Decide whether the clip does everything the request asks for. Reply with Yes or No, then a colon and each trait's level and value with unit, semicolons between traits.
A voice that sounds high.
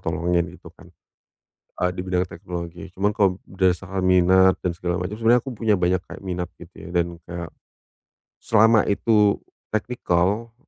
No: very low, 95 Hz